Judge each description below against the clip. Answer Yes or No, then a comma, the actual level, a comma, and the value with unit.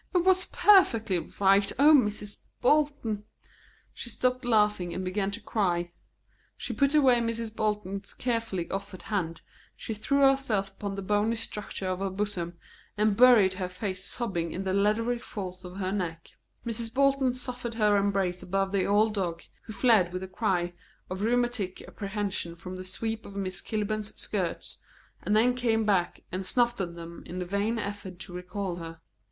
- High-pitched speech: Yes, high, 205 Hz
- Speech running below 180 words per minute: Yes, average, 170 wpm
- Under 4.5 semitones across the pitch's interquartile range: Yes, average, 3.6 semitones